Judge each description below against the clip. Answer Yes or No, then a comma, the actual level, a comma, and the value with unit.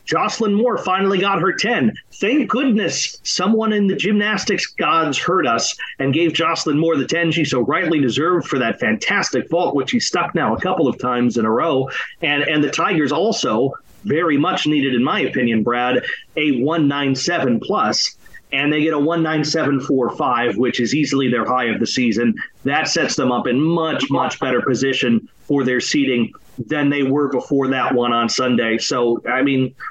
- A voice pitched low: No, medium, 145 Hz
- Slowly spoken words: No, average, 195 wpm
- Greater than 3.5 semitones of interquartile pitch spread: Yes, average, 5.1 semitones